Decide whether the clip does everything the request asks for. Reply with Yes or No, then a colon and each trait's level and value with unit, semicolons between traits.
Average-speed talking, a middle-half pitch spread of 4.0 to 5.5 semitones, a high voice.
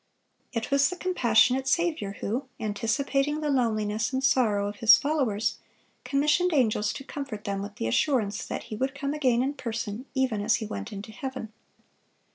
Yes: average, 175 wpm; average, 4.5 semitones; high, 245 Hz